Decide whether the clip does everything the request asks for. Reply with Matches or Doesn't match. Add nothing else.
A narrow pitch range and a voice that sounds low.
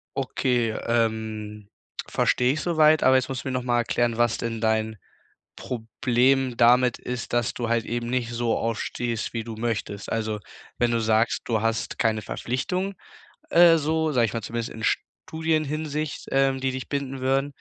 Doesn't match